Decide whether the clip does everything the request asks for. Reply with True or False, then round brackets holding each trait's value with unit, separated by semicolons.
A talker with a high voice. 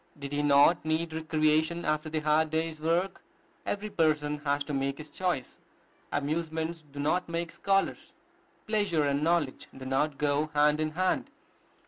False (155 Hz)